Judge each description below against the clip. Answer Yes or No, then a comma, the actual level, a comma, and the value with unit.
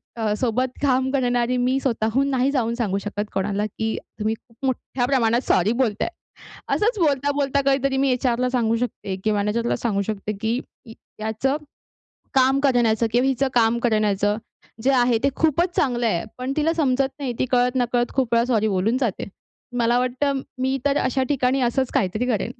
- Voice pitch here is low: No, high, 245 Hz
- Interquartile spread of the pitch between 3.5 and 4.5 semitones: No, average, 3.1 semitones